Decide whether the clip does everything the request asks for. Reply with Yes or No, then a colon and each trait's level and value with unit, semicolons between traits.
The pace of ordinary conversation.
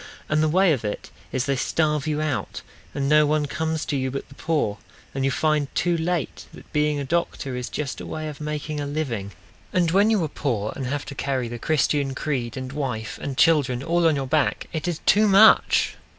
No: fast, 220 wpm